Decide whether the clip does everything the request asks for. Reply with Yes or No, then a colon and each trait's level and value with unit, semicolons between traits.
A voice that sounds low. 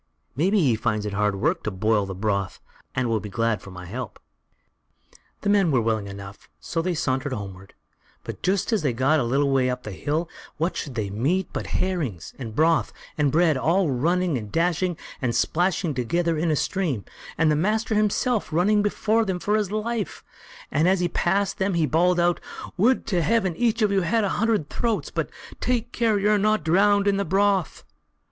No: medium, 165 Hz